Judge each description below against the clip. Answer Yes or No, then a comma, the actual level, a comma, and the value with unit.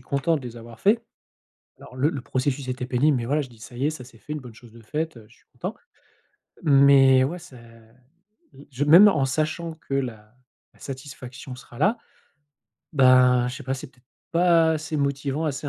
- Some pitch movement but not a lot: Yes, average, 3.3 semitones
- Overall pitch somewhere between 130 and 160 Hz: Yes, low, 135 Hz